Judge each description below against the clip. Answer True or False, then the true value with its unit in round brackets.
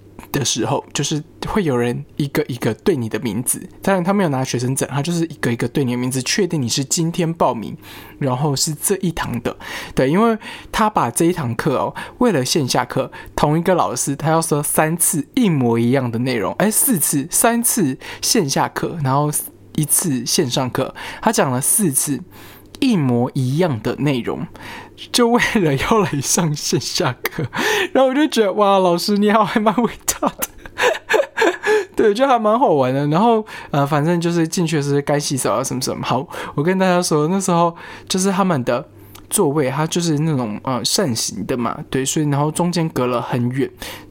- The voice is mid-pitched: True (155 Hz)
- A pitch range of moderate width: False (6.3 semitones)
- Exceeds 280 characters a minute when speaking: False (270 characters per minute)